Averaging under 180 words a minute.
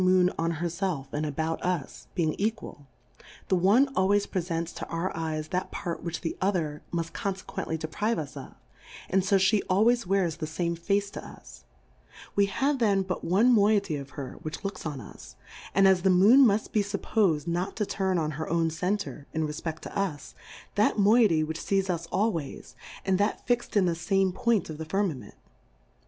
No: average, 190 wpm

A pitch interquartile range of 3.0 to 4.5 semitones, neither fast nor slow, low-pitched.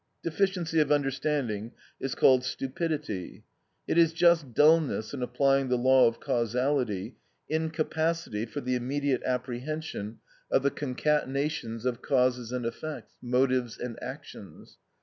No: average, 3.7 semitones; slow, 125 wpm; low, 130 Hz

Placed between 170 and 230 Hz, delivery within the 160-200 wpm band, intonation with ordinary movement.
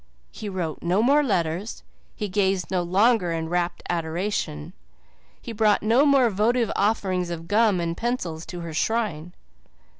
No: high, 190 Hz; average, 150 wpm; average, 4.5 semitones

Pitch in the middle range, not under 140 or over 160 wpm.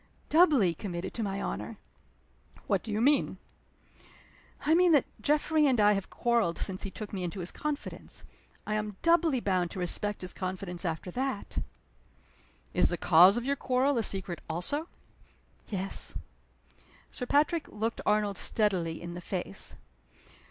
No: high, 210 Hz; average, 150 wpm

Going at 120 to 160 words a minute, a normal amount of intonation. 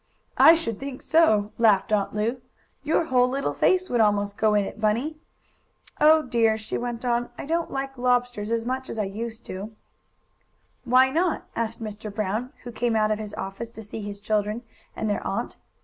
No: average, 190 wpm; average, 3.3 semitones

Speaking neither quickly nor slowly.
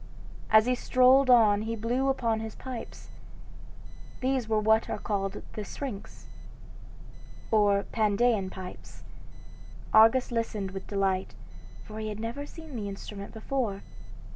No: slow, 130 wpm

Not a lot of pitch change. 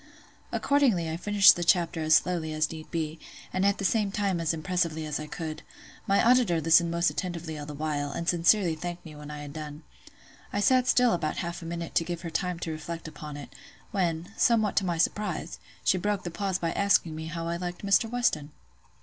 No: average, 3.6 semitones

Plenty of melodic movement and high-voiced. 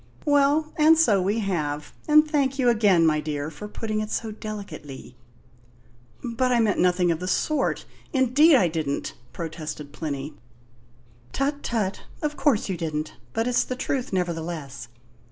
Yes: wide, 8.5 semitones; high, 205 Hz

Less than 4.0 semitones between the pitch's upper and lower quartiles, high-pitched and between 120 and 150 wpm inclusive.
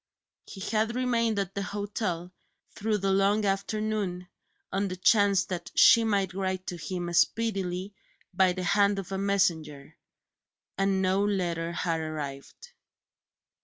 Yes: narrow, 2.5 semitones; high, 195 Hz; slow, 135 wpm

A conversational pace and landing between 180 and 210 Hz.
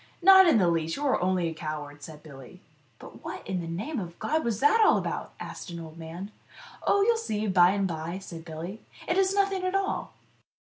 No: fast, 235 wpm; medium, 185 Hz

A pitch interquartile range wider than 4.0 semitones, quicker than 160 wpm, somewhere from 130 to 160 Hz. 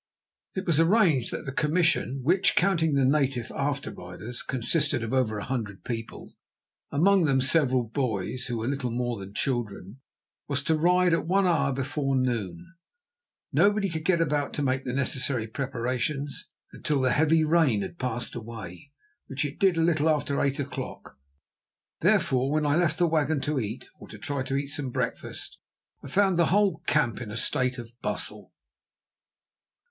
Yes: average, 4.5 semitones; average, 170 wpm; medium, 140 Hz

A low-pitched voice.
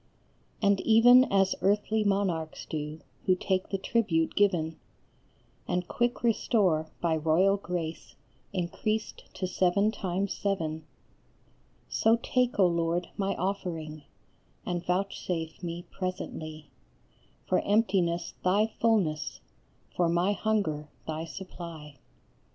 No: medium, 180 Hz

